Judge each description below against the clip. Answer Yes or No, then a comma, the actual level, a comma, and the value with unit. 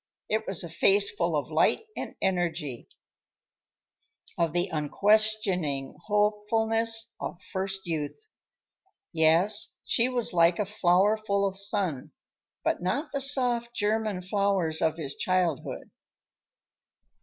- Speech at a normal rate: No, slow, 120 wpm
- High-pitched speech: Yes, high, 195 Hz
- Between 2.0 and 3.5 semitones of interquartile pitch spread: No, average, 4.3 semitones